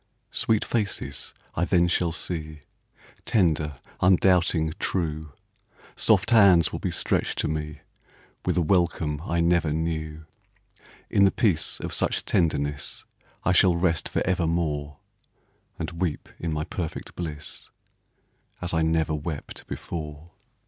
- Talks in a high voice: No, very low, 80 Hz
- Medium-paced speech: No, slow, 125 wpm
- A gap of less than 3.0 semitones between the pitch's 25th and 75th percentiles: Yes, narrow, 2.5 semitones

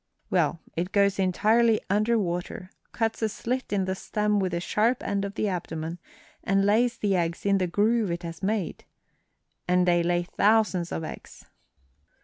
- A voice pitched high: Yes, high, 195 Hz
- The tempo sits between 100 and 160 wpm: No, average, 170 wpm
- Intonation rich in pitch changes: No, average, 3.4 semitones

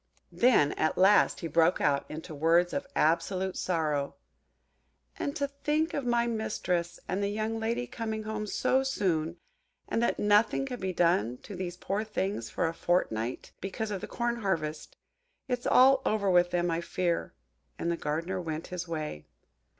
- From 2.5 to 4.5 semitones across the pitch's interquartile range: No, average, 5.1 semitones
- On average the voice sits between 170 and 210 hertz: Yes, medium, 185 Hz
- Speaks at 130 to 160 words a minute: No, average, 170 wpm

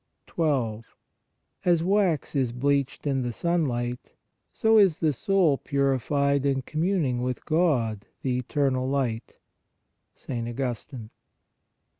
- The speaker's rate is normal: No, slow, 110 wpm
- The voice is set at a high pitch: No, medium, 140 Hz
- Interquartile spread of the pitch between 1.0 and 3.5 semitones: No, average, 4.2 semitones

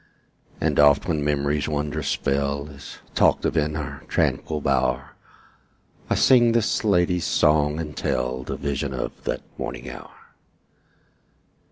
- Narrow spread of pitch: Yes, narrow, 1.8 semitones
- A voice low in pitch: Yes, very low, 75 Hz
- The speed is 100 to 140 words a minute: Yes, slow, 135 wpm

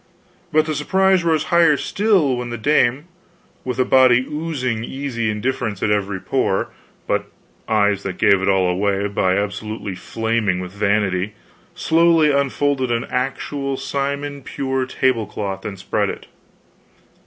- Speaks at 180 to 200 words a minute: No, average, 140 wpm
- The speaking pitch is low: Yes, low, 125 Hz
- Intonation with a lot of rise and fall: Yes, wide, 5.7 semitones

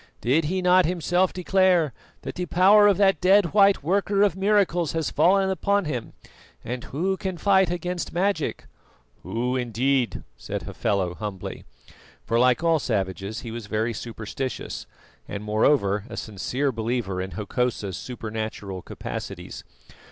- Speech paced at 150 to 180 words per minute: No, average, 140 wpm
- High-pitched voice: No, medium, 140 Hz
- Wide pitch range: Yes, wide, 8.9 semitones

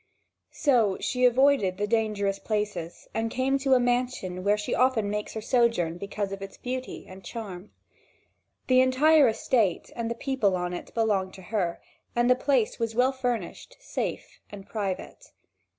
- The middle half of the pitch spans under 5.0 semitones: Yes, average, 4.3 semitones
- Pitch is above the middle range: Yes, high, 225 Hz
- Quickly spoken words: No, average, 165 wpm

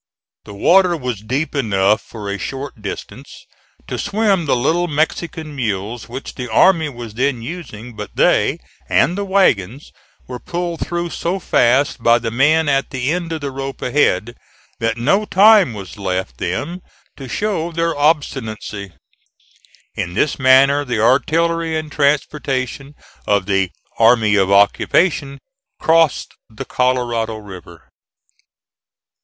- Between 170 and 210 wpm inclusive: No, average, 140 wpm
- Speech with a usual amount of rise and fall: No, wide, 6.4 semitones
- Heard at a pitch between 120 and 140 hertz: Yes, low, 135 Hz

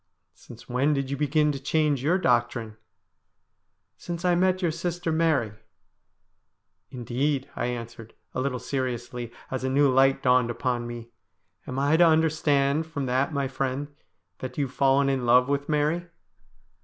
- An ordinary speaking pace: Yes, average, 175 wpm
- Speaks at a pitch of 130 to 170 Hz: Yes, low, 135 Hz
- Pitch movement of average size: Yes, average, 3.3 semitones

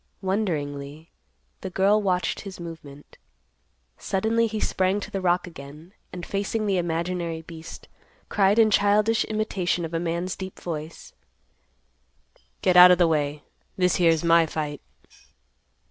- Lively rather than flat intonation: No, average, 3.2 semitones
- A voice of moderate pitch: Yes, medium, 180 Hz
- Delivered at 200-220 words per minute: No, slow, 135 wpm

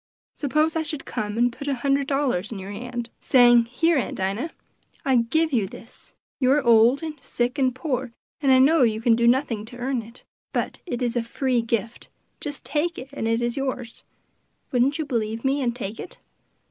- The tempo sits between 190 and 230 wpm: Yes, fast, 205 wpm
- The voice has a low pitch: No, very high, 250 Hz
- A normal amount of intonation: Yes, average, 3.2 semitones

